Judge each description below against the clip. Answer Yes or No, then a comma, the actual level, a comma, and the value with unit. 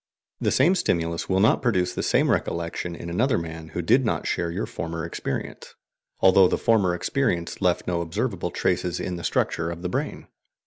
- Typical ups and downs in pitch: No, narrow, 2.1 semitones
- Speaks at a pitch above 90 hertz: No, very low, 85 Hz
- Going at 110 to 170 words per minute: No, average, 185 wpm